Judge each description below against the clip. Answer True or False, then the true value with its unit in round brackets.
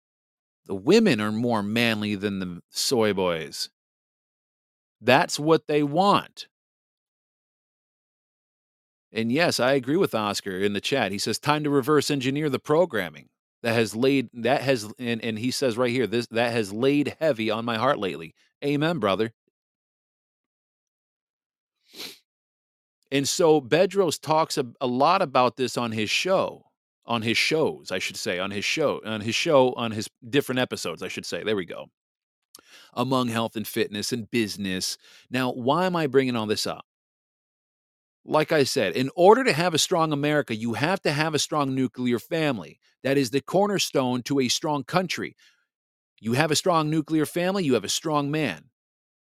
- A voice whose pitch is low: True (130 Hz)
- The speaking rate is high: False (165 wpm)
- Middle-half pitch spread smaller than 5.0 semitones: True (4.5 semitones)